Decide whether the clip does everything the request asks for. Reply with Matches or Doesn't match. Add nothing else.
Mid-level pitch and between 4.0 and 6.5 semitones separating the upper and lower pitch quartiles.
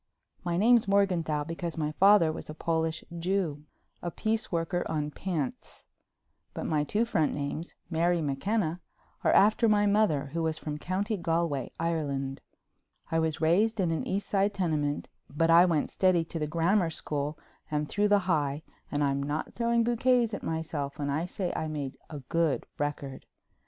Matches